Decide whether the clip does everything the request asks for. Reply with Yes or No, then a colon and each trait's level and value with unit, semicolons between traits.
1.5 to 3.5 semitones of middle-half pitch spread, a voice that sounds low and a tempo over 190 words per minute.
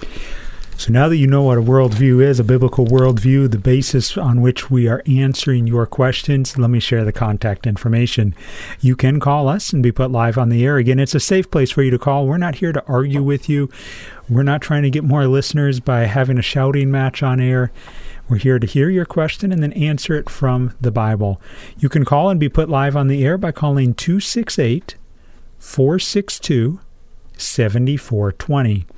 Yes: average, 2.9 semitones; low, 130 Hz; average, 200 wpm